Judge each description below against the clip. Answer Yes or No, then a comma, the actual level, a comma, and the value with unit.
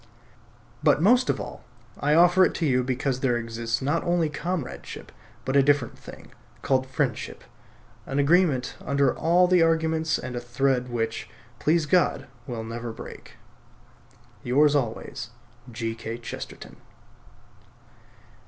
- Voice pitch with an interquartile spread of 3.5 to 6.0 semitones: Yes, average, 4.9 semitones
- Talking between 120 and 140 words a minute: Yes, slow, 135 wpm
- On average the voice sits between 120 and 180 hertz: Yes, low, 135 Hz